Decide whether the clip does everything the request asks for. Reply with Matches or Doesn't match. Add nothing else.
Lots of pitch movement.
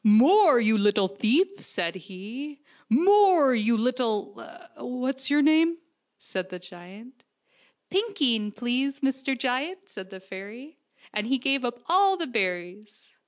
Matches